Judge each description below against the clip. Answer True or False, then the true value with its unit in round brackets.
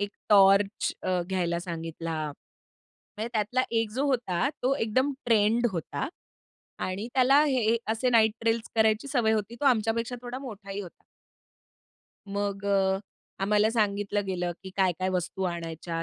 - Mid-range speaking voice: False (210 Hz)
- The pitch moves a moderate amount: True (3.5 semitones)